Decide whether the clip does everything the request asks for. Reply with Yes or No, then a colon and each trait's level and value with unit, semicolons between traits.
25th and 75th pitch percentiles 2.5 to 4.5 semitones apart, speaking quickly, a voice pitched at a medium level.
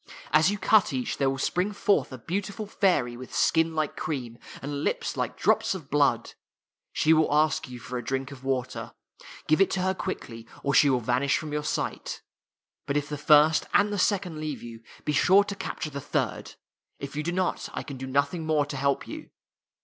No: average, 5.0 semitones; fast, 210 wpm; medium, 150 Hz